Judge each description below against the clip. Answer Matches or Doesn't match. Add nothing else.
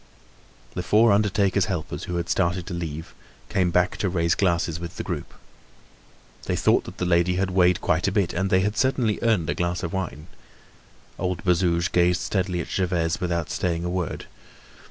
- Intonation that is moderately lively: Doesn't match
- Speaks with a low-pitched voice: Matches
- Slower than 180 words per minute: Doesn't match